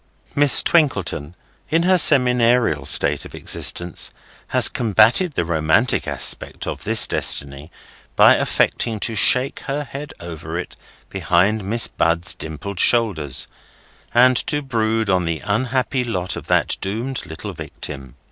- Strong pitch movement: Yes, wide, 6.8 semitones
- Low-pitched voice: Yes, low, 110 Hz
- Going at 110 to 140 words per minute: Yes, slow, 135 wpm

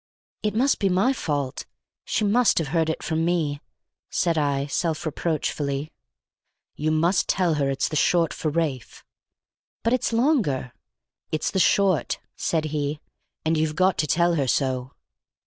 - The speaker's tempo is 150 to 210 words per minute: Yes, average, 155 wpm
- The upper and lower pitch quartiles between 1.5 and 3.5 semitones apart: No, average, 4.0 semitones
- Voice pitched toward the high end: No, medium, 160 Hz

